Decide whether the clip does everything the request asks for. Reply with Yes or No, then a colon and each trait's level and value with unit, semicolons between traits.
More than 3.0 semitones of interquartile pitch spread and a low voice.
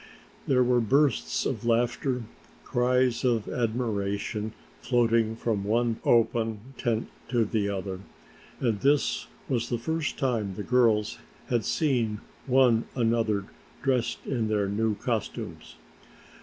No: narrow, 2.5 semitones; low, 115 Hz